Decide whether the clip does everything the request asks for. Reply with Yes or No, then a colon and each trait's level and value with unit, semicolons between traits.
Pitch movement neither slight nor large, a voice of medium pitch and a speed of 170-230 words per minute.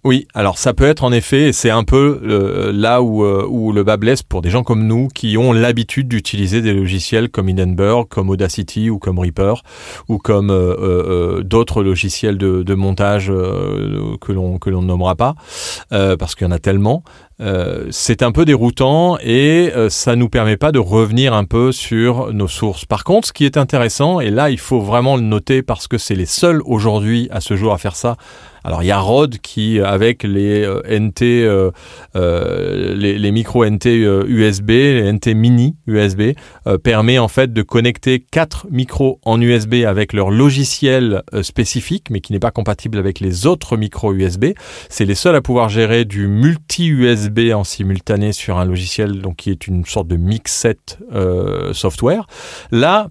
No: average, 3.9 semitones; low, 110 Hz; average, 195 wpm